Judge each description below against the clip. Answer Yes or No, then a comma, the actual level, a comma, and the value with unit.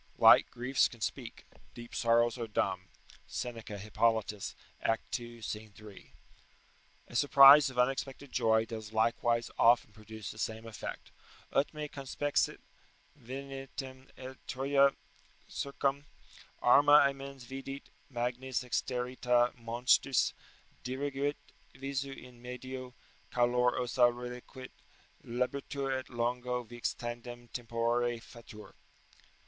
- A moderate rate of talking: No, slow, 110 wpm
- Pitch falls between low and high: No, low, 125 Hz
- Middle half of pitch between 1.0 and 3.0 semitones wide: Yes, narrow, 2.4 semitones